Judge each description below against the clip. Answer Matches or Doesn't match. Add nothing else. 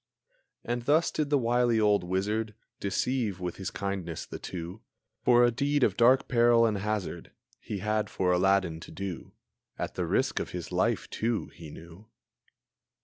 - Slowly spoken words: Doesn't match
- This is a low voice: Matches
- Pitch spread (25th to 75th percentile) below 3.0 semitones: Doesn't match